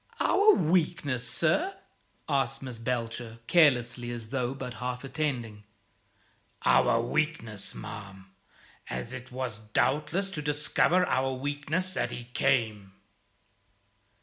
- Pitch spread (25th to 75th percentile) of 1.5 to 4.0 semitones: No, average, 4.5 semitones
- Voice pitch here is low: Yes, low, 130 Hz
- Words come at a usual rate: No, slow, 110 wpm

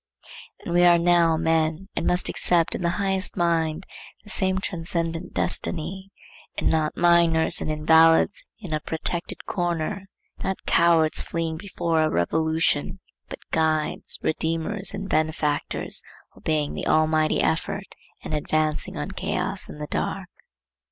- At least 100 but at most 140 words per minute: Yes, slow, 135 wpm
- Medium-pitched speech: Yes, medium, 165 Hz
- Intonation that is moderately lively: No, narrow, 1.9 semitones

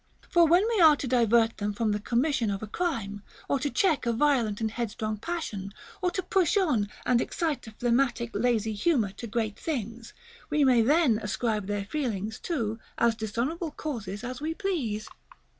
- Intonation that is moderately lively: No, wide, 6.0 semitones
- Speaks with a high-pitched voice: Yes, high, 235 Hz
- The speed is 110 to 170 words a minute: No, average, 180 wpm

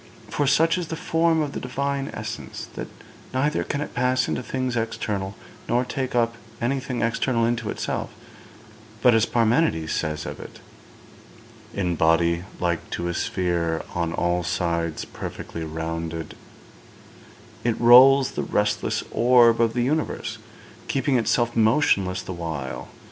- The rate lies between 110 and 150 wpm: Yes, average, 140 wpm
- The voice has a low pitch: Yes, low, 115 Hz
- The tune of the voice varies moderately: No, wide, 6.9 semitones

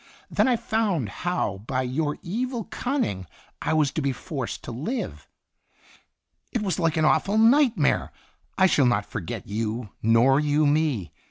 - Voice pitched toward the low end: No, medium, 155 Hz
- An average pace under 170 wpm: Yes, average, 160 wpm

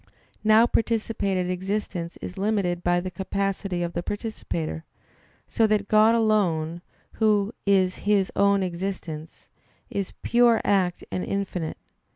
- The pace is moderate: No, slow, 125 wpm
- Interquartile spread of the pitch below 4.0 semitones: Yes, average, 3.2 semitones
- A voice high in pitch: Yes, high, 195 Hz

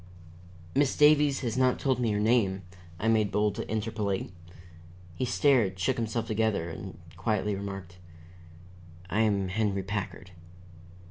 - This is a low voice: Yes, low, 105 Hz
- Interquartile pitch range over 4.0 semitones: No, average, 3.2 semitones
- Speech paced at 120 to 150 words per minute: Yes, slow, 135 wpm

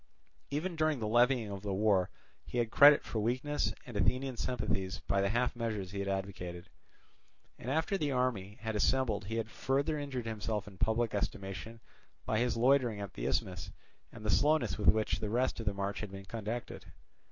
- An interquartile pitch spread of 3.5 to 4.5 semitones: Yes, average, 4.1 semitones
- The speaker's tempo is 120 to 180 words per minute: No, average, 190 wpm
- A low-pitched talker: Yes, low, 110 Hz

